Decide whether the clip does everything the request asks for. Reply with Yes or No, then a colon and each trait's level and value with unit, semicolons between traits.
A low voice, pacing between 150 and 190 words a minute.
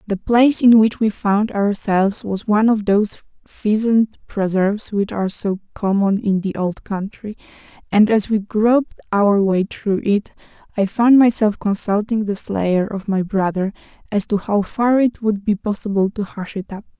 No: high, 205 Hz; average, 175 wpm